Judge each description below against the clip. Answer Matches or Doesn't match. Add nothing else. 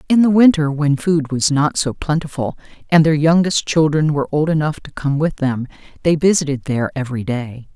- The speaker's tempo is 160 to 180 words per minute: Doesn't match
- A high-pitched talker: Doesn't match